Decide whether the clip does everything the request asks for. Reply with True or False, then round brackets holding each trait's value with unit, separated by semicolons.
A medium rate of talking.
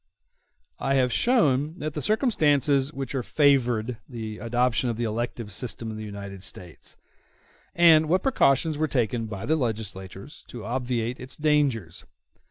True (150 wpm)